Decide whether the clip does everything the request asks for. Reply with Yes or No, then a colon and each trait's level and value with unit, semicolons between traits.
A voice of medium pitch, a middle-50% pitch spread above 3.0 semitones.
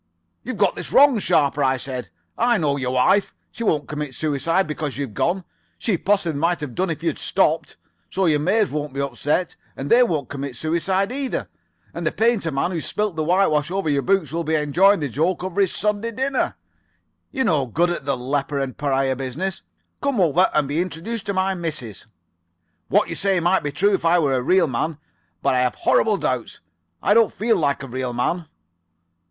Yes: medium, 165 Hz; wide, 5.5 semitones